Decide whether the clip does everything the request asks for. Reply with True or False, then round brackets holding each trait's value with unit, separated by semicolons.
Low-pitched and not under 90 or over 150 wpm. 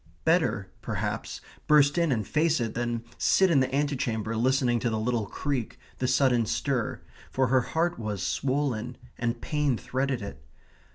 False (125 Hz; 160 wpm)